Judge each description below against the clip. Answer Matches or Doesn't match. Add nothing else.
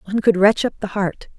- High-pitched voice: Matches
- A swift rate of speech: Matches